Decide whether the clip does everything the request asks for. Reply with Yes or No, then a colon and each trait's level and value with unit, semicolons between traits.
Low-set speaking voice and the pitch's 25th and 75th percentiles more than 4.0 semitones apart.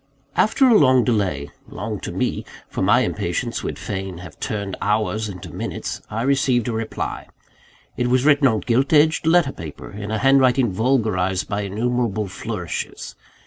Yes: low, 115 Hz; average, 4.8 semitones